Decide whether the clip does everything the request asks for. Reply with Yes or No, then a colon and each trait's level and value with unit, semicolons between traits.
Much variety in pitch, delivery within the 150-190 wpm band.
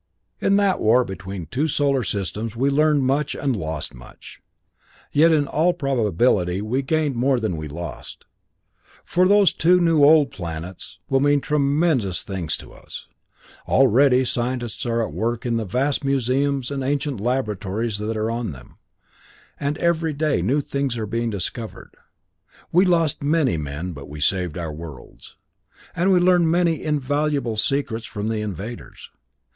Yes: wide, 6.1 semitones; average, 155 wpm